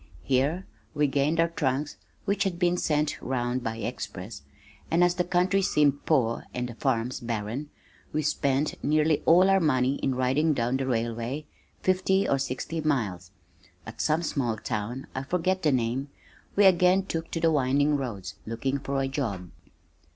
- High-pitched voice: No, medium, 140 Hz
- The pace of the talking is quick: No, average, 165 wpm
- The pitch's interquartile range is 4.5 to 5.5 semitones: Yes, average, 5.0 semitones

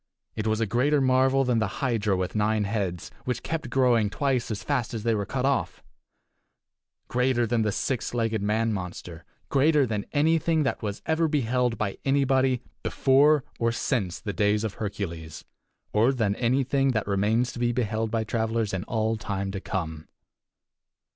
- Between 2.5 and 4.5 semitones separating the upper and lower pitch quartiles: Yes, average, 4.1 semitones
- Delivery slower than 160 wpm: No, average, 170 wpm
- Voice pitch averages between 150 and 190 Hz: No, low, 115 Hz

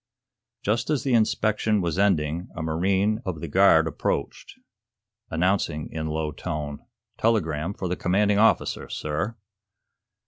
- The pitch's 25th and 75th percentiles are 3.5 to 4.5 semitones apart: No, average, 4.9 semitones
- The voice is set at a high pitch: No, very low, 90 Hz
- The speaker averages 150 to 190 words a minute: No, slow, 135 wpm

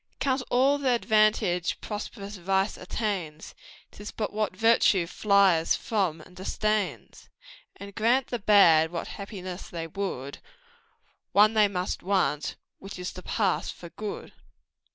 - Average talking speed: No, slow, 130 wpm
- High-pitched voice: Yes, high, 200 Hz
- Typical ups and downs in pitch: Yes, average, 3.1 semitones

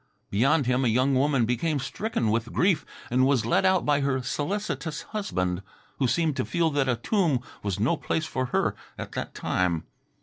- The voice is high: No, low, 135 Hz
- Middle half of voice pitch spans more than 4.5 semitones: Yes, average, 5.0 semitones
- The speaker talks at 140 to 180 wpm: No, average, 190 wpm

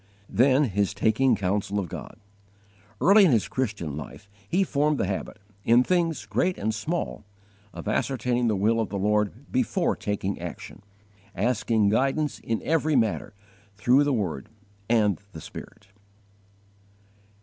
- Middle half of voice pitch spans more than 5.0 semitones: Yes, wide, 5.5 semitones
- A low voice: Yes, low, 110 Hz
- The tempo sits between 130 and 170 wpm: Yes, average, 145 wpm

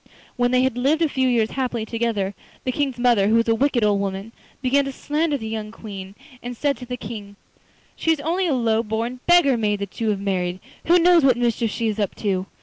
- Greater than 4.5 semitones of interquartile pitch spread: No, average, 4.1 semitones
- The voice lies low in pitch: No, high, 235 Hz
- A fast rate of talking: Yes, fast, 235 wpm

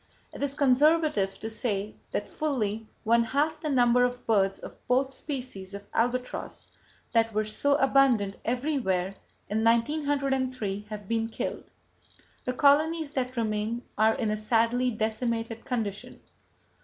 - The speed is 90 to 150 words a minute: Yes, average, 145 wpm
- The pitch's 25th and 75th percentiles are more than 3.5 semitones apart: Yes, average, 3.9 semitones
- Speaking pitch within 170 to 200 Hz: No, high, 235 Hz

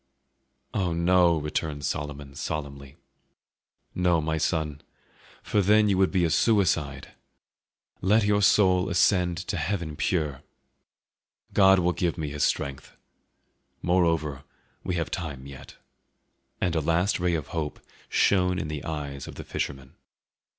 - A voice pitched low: Yes, very low, 80 Hz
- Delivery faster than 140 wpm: No, slow, 135 wpm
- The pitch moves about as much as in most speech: Yes, average, 3.8 semitones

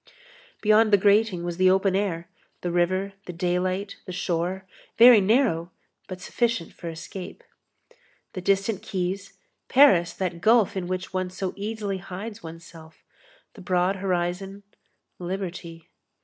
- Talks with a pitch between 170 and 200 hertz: Yes, medium, 185 Hz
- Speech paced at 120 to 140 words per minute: Yes, slow, 135 wpm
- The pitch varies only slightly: Yes, narrow, 2.2 semitones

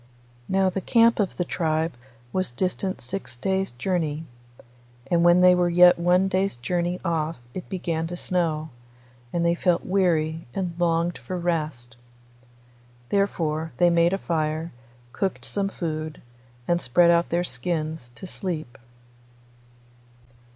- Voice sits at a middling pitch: Yes, medium, 170 Hz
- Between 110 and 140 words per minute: Yes, slow, 135 wpm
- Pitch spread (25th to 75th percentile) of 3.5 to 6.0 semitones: No, narrow, 2.5 semitones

